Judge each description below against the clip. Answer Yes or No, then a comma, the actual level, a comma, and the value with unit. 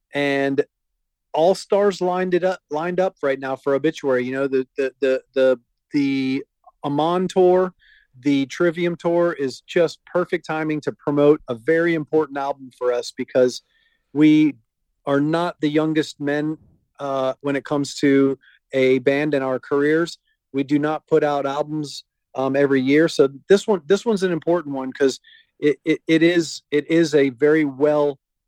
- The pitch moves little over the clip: No, average, 3.6 semitones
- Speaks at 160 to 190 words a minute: Yes, average, 170 wpm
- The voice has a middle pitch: Yes, medium, 150 Hz